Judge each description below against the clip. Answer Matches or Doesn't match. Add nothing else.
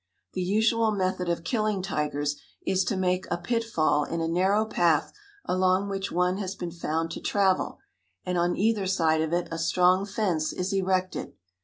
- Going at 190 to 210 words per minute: Doesn't match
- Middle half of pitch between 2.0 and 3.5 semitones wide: Matches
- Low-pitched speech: Doesn't match